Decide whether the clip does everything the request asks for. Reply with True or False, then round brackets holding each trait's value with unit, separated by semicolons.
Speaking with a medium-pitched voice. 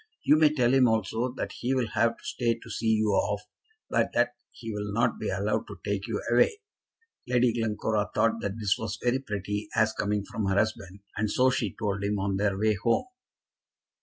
False (110 Hz)